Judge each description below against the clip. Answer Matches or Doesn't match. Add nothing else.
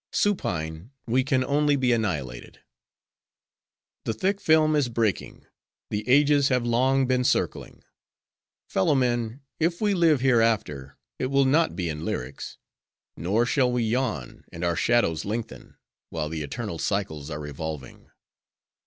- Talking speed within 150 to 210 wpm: Doesn't match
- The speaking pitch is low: Matches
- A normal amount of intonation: Doesn't match